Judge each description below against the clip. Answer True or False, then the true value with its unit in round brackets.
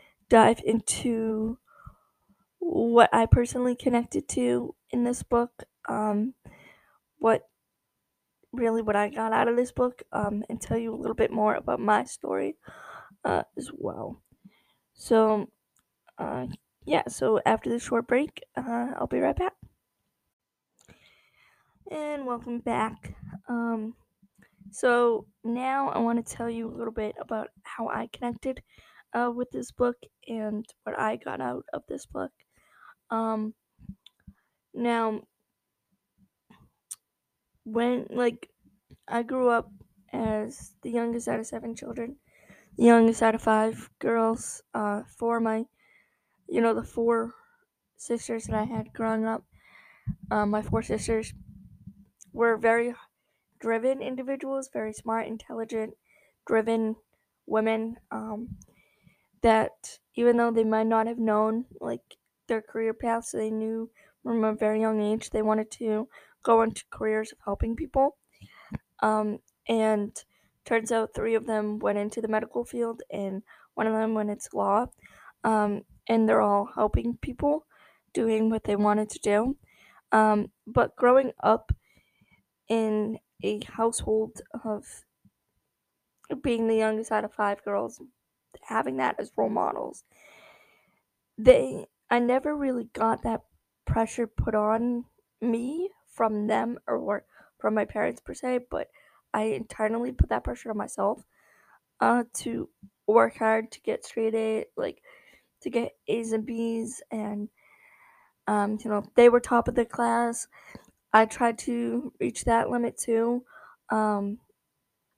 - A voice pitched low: False (225 Hz)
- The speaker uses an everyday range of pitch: False (1.7 semitones)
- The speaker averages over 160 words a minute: False (135 wpm)